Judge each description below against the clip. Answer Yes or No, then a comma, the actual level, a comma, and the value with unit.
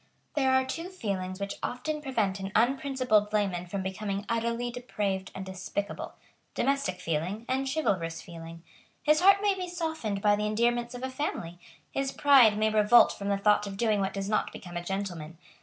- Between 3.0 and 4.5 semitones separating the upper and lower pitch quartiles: No, average, 5.3 semitones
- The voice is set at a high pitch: Yes, high, 210 Hz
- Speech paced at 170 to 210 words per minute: Yes, average, 180 wpm